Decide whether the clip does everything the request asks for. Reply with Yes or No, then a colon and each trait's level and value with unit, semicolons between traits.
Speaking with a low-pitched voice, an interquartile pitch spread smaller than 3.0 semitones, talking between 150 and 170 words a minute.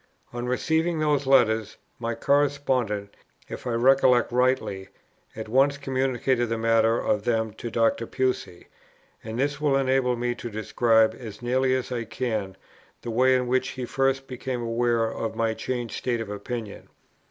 Yes: low, 120 Hz; narrow, 2.5 semitones; average, 160 wpm